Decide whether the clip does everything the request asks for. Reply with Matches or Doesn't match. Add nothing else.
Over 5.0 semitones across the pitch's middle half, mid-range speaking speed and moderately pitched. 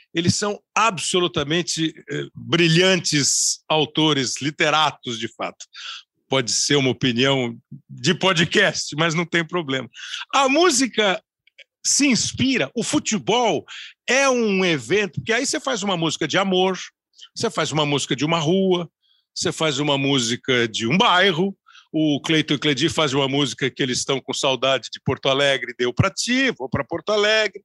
Matches